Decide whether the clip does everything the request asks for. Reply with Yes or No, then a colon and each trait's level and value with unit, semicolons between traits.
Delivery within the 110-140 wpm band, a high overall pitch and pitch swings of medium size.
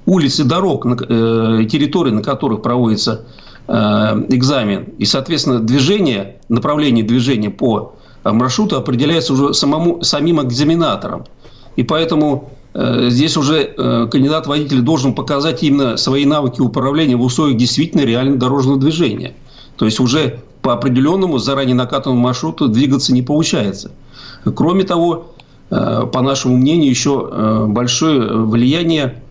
No: average, 115 wpm; low, 135 Hz; average, 3.5 semitones